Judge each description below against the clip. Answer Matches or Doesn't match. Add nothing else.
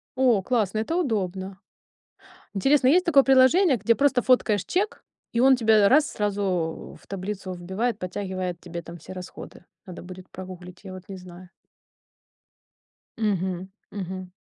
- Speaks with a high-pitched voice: Matches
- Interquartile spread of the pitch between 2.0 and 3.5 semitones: Doesn't match